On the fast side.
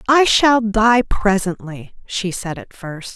No: average, 150 wpm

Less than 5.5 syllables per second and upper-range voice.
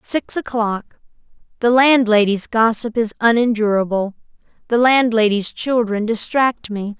Yes: 4.4 syllables/s; high, 225 Hz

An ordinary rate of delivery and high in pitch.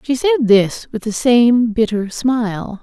Yes: average, 170 wpm; high, 230 Hz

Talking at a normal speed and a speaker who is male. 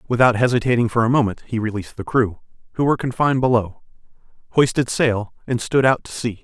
Yes: average, 185 wpm; male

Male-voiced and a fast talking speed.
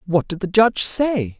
No: female; fast, 215 wpm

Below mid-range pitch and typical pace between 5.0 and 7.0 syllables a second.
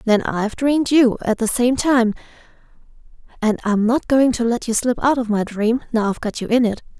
No: high, 235 Hz; 5.5 syllables/s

